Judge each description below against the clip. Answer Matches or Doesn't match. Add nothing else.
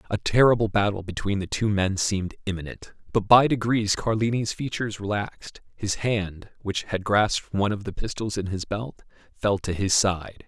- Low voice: Matches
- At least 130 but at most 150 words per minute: Doesn't match